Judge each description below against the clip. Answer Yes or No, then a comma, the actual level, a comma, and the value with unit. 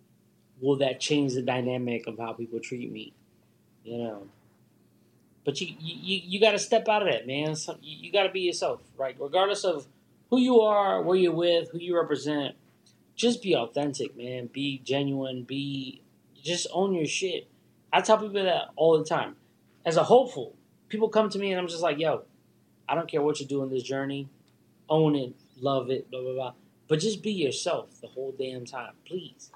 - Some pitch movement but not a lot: No, wide, 5.8 semitones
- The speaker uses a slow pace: No, average, 200 wpm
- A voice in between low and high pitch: Yes, medium, 150 Hz